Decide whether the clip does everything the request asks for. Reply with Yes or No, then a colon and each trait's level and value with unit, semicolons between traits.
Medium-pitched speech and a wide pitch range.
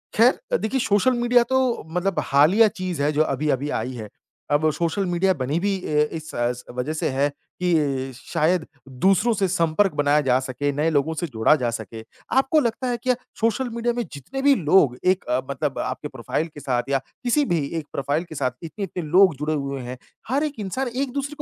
Yes: medium, 160 Hz; wide, 7.3 semitones